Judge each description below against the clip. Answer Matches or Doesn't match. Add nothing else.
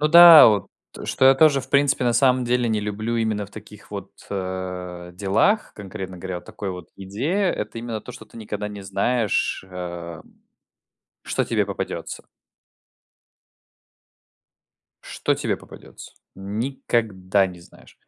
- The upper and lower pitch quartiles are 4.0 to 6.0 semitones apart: Matches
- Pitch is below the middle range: Matches